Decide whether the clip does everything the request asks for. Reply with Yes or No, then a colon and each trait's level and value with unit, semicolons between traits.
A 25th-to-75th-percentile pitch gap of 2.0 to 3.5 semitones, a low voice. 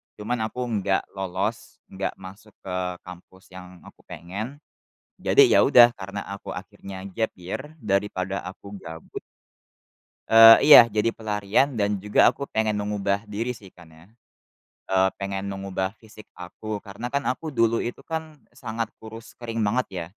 Yes: average, 3.1 semitones; low, 105 Hz